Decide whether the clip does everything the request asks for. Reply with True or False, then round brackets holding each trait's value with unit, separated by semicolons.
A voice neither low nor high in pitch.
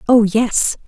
False (225 Hz)